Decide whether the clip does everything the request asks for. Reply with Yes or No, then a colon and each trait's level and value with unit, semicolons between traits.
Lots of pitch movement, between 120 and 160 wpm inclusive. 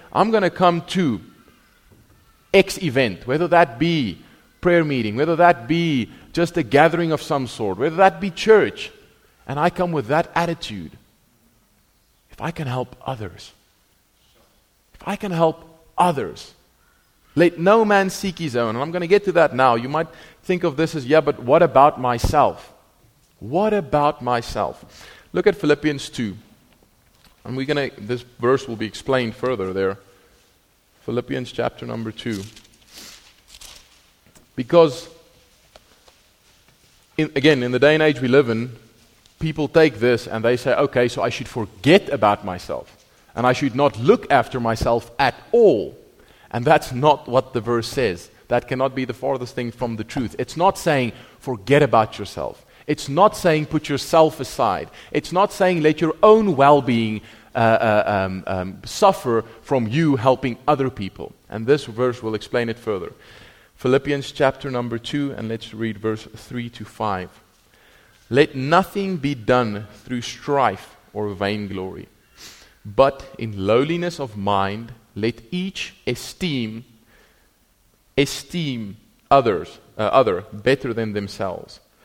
Yes: wide, 5.8 semitones; average, 150 wpm